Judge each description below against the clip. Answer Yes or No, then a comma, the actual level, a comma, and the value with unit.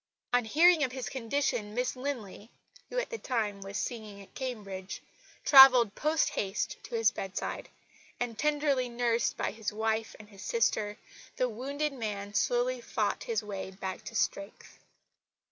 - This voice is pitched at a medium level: No, high, 230 Hz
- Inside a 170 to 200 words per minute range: No, average, 155 wpm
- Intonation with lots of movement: No, average, 3.8 semitones